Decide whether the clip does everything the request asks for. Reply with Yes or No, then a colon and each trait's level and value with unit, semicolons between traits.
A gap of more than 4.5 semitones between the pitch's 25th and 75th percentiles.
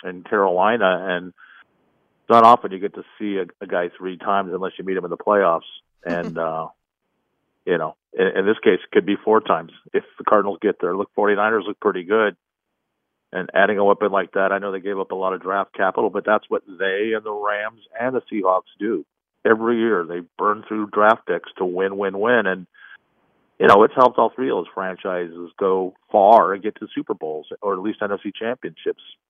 No: average, 2.7 semitones